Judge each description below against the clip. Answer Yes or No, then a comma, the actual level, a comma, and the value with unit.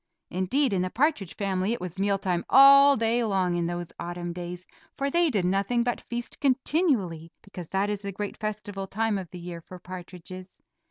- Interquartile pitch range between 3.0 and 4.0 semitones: No, average, 4.8 semitones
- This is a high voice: Yes, high, 195 Hz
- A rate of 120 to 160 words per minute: No, average, 195 wpm